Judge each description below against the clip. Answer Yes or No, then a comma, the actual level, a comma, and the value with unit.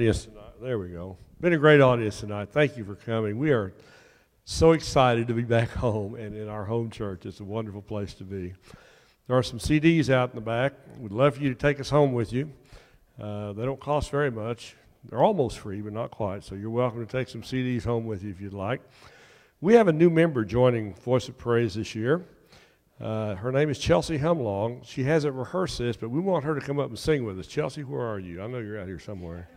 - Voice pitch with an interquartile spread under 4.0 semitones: No, average, 4.6 semitones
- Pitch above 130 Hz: No, low, 120 Hz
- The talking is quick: Yes, fast, 235 wpm